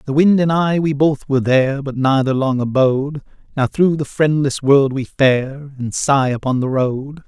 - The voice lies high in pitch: No, medium, 140 Hz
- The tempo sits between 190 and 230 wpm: Yes, average, 200 wpm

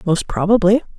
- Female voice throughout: Yes, female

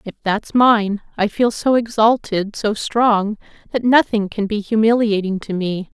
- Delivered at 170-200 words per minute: No, average, 160 wpm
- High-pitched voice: Yes, high, 215 Hz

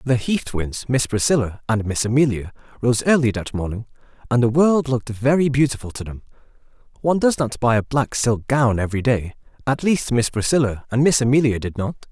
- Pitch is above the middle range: No, low, 125 Hz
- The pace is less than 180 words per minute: No, average, 190 wpm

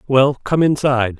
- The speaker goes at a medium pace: Yes, average, 150 wpm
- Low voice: Yes, low, 130 Hz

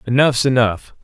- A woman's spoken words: No, male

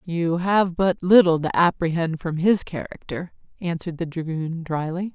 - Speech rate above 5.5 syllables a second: No, 4.6 syllables/s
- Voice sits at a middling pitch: Yes, medium, 170 Hz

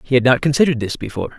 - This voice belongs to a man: Yes, male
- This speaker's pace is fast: Yes, fast, 260 wpm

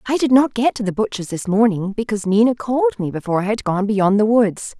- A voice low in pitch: No, high, 215 Hz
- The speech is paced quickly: Yes, fast, 250 wpm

